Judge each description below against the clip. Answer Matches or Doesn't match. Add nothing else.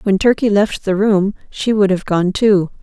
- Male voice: Doesn't match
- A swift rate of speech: Matches